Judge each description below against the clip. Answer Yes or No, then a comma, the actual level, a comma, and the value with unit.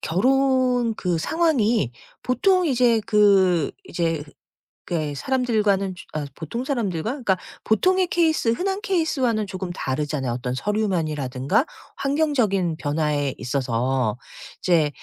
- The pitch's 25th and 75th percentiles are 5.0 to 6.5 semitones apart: No, wide, 8.8 semitones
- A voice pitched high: Yes, high, 200 Hz